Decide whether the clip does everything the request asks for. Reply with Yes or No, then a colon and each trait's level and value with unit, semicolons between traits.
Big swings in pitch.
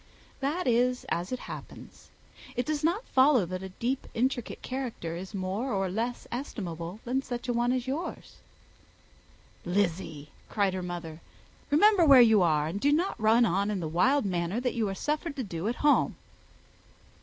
Yes: wide, 6.1 semitones